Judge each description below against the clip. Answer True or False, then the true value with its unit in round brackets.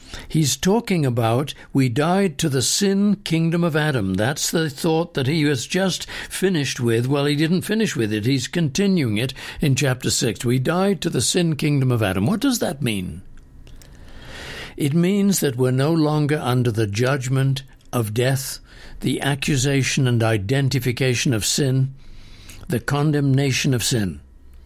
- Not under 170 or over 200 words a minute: False (160 wpm)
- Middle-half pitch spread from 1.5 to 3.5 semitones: False (5.1 semitones)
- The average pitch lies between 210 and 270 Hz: False (135 Hz)